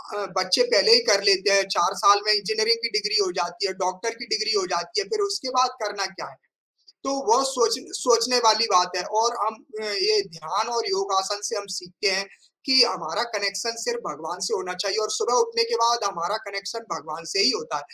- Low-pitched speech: No, high, 225 Hz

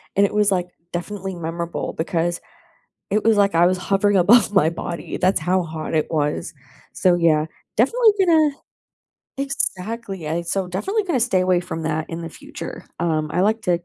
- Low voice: No, medium, 185 Hz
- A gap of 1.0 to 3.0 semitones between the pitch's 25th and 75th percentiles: No, average, 3.8 semitones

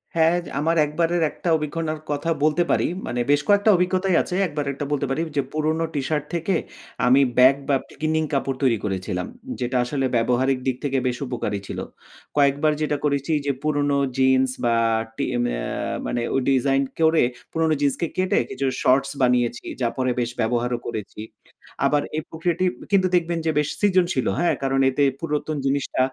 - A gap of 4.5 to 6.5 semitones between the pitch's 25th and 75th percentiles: No, average, 3.7 semitones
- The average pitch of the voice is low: No, medium, 145 Hz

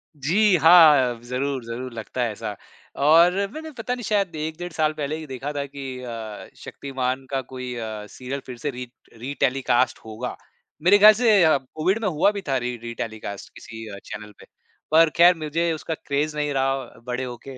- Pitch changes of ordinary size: Yes, average, 4.7 semitones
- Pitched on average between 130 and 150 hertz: Yes, medium, 140 Hz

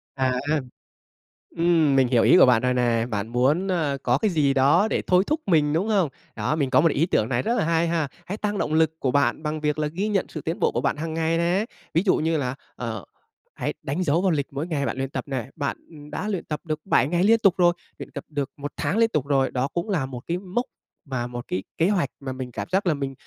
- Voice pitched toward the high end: No, medium, 150 Hz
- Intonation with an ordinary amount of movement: Yes, average, 4.6 semitones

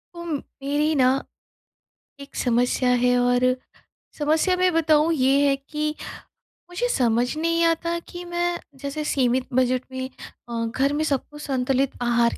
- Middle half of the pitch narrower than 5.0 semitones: Yes, average, 4.0 semitones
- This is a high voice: Yes, very high, 280 Hz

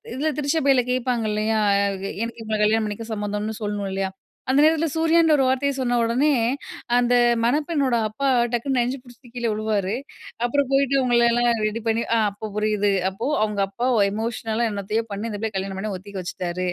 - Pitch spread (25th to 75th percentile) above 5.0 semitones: No, average, 3.7 semitones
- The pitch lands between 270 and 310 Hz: No, high, 230 Hz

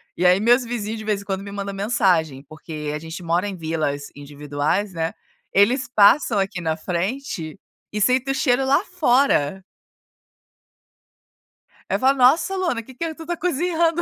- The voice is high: Yes, high, 205 Hz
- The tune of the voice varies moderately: No, wide, 8.0 semitones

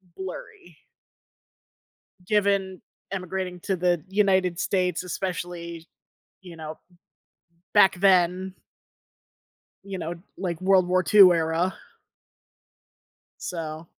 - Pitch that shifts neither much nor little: No, narrow, 1.9 semitones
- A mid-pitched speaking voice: Yes, medium, 180 Hz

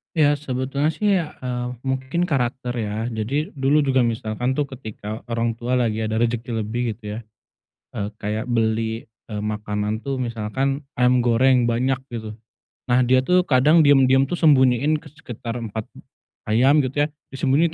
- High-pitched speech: No, low, 125 Hz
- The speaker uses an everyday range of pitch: Yes, average, 3.4 semitones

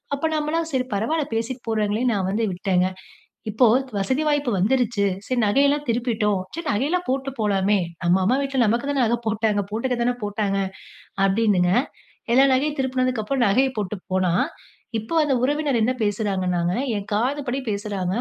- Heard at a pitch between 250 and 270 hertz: No, high, 230 Hz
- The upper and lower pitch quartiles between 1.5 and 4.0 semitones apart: No, average, 4.7 semitones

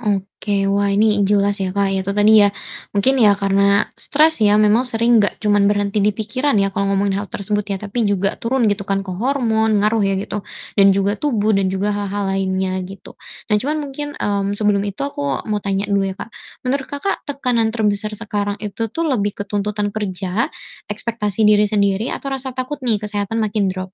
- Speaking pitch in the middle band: No, high, 210 Hz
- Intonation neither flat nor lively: No, narrow, 2.3 semitones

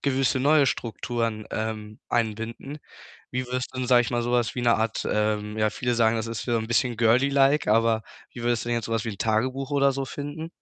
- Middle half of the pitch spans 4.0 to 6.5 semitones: No, average, 2.7 semitones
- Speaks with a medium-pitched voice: No, low, 120 Hz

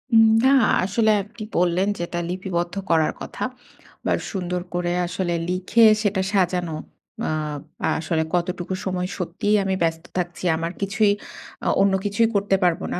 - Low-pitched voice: No, medium, 180 Hz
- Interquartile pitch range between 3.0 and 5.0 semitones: No, narrow, 2.4 semitones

